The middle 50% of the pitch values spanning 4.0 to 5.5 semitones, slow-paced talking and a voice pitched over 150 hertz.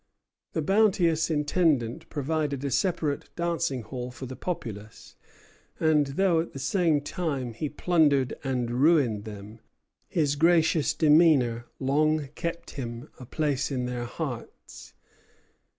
No: average, 4.5 semitones; slow, 125 wpm; medium, 145 Hz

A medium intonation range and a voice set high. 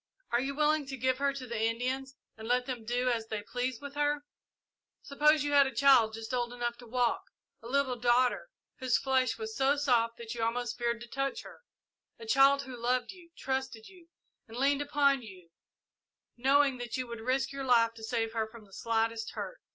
Yes: average, 3.1 semitones; very high, 250 Hz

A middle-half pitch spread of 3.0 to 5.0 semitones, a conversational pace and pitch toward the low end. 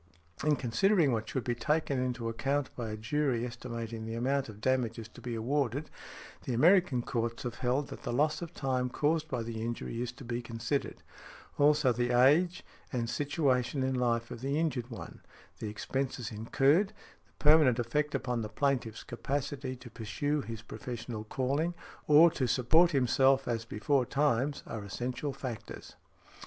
Yes: average, 3.5 semitones; average, 165 wpm; low, 125 Hz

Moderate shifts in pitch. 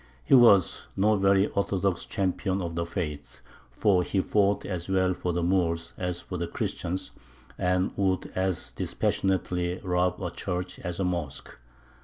No: narrow, 1.7 semitones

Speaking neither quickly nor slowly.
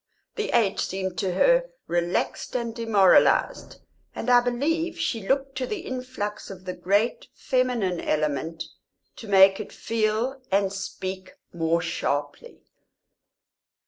No: slow, 125 wpm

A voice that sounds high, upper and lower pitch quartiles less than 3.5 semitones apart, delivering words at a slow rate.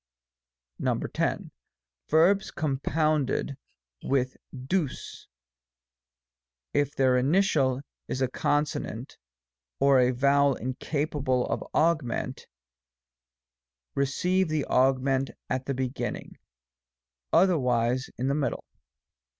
No: low, 135 Hz; average, 3.0 semitones; slow, 85 wpm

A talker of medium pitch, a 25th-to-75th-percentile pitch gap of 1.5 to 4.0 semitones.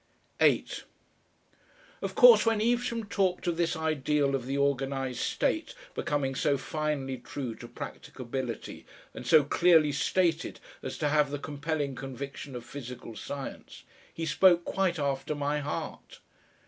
Yes: medium, 145 Hz; average, 3.5 semitones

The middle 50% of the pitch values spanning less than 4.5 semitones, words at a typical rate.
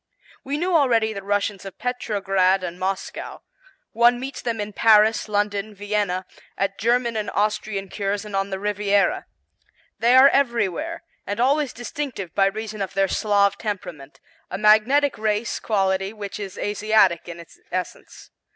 Yes: average, 2.9 semitones; average, 150 wpm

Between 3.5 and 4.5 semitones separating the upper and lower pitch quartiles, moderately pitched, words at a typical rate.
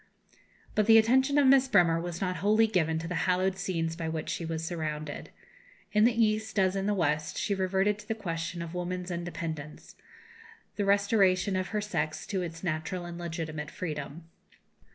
Yes: average, 3.9 semitones; medium, 180 Hz; average, 180 wpm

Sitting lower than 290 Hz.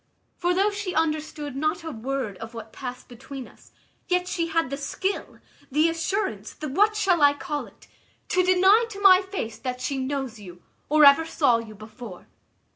No: very high, 295 Hz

